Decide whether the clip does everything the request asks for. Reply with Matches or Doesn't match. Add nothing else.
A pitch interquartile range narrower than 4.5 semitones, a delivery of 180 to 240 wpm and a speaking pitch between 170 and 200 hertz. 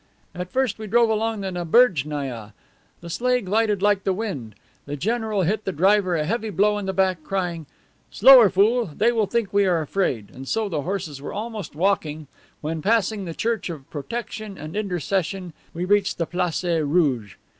Doesn't match